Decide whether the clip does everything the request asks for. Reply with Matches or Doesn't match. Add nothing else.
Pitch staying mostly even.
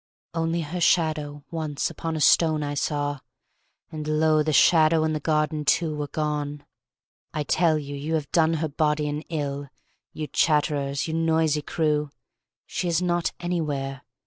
Matches